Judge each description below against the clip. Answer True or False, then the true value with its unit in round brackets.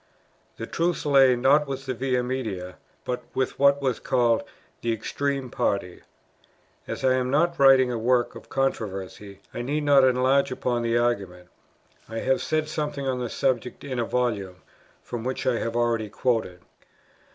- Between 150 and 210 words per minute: True (165 wpm)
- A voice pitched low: True (125 Hz)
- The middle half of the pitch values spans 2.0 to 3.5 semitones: True (2.9 semitones)